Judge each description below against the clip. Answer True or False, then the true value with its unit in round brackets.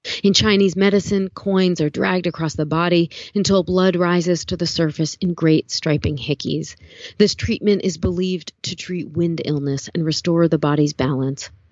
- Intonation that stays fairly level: False (3.7 semitones)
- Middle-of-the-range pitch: True (170 Hz)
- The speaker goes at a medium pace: True (165 wpm)